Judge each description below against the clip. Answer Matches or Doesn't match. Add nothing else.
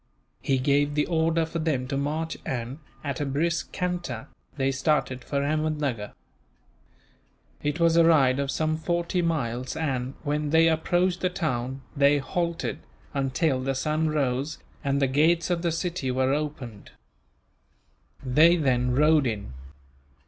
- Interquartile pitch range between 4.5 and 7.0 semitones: Doesn't match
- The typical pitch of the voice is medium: Matches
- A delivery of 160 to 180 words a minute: Doesn't match